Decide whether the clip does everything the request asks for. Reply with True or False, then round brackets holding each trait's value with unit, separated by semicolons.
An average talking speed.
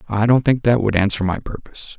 False (240 wpm)